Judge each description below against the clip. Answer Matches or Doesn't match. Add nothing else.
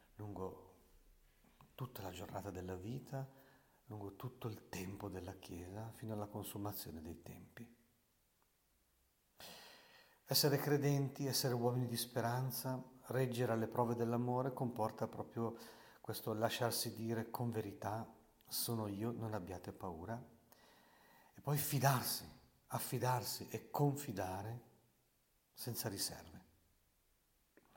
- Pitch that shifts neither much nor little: Matches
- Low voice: Matches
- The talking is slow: Matches